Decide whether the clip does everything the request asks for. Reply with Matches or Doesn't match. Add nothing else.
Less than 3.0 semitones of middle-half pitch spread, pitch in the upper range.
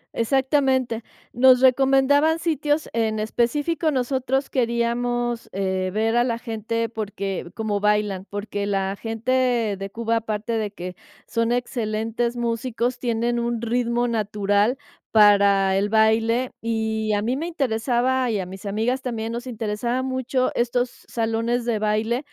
Matches